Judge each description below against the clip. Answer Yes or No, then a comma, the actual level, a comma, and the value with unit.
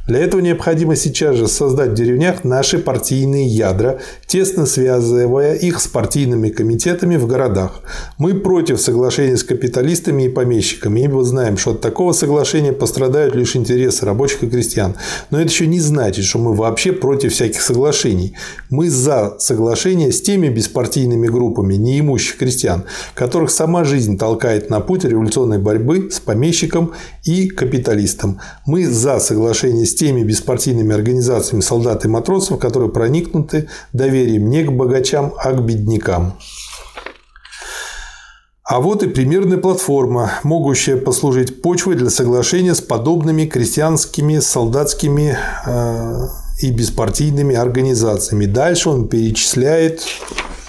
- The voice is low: Yes, low, 130 Hz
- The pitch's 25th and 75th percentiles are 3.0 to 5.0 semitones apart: No, wide, 5.5 semitones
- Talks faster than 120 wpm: Yes, average, 130 wpm